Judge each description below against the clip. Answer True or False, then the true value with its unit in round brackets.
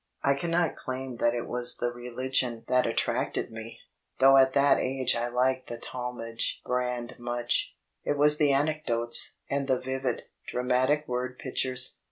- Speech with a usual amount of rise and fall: False (1.8 semitones)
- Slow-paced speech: False (155 wpm)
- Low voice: True (125 Hz)